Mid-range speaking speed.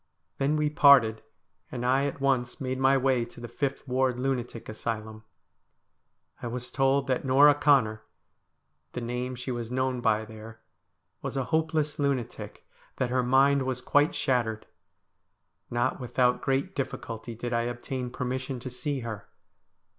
Yes: average, 155 wpm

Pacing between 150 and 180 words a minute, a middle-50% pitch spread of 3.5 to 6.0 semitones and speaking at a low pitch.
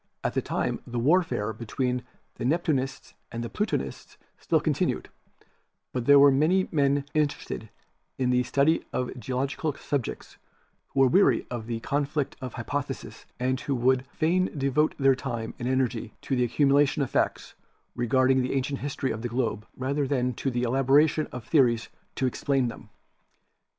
No: average, 160 wpm; narrow, 2.5 semitones; low, 130 Hz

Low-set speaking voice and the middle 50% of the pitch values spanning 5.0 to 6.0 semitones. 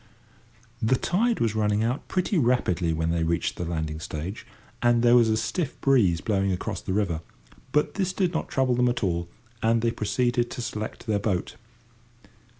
Yes: low, 110 Hz; wide, 5.5 semitones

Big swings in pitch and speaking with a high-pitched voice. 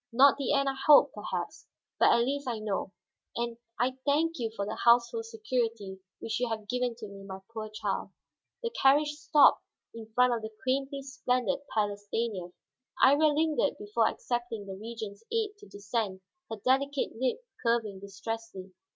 No: average, 4.5 semitones; high, 235 Hz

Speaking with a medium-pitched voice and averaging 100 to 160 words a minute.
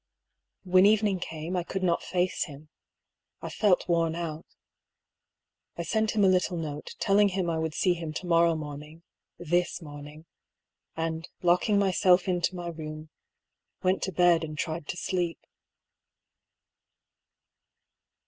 Yes: medium, 170 Hz; average, 140 wpm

